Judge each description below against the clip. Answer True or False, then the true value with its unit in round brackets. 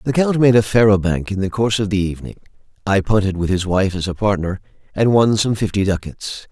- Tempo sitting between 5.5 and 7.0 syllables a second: True (5.9 syllables/s)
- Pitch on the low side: True (100 Hz)